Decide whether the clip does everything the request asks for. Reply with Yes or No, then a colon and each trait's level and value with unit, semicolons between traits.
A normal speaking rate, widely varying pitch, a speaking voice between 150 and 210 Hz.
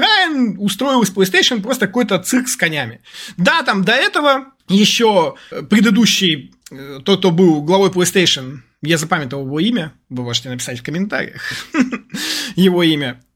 Yes: average, 130 wpm; wide, 7.6 semitones; high, 190 Hz